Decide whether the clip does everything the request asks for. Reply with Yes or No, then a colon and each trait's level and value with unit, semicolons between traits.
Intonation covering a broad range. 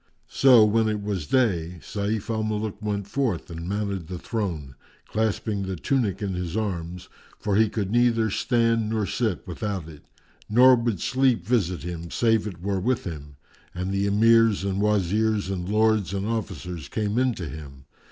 No: average, 3.6 semitones